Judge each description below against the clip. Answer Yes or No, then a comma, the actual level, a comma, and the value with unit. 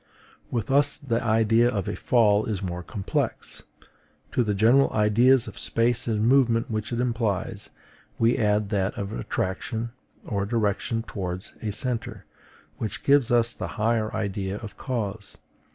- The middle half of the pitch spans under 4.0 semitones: Yes, average, 2.7 semitones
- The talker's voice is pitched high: No, low, 110 Hz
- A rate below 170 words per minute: Yes, average, 150 wpm